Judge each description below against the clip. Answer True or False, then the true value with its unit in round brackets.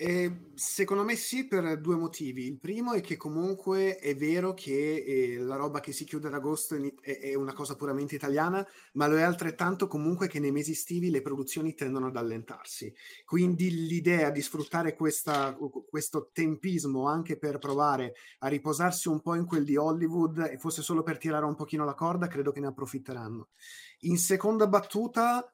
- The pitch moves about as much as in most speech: True (3.6 semitones)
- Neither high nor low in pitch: True (155 Hz)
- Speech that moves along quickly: True (180 wpm)